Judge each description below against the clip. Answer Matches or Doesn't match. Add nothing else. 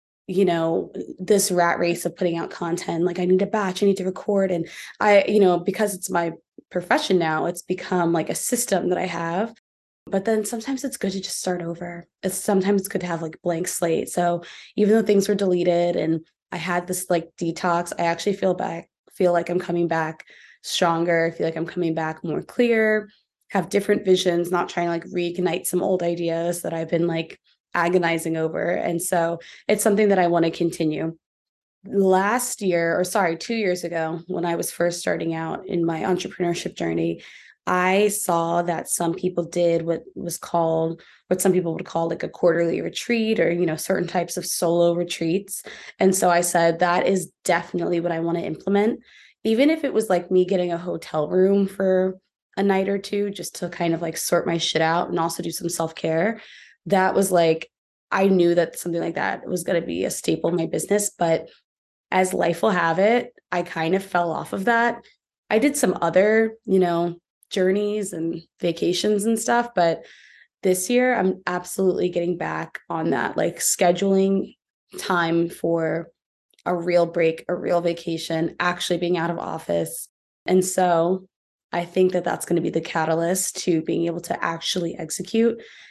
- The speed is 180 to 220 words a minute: Matches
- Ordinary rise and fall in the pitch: Doesn't match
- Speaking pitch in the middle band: Matches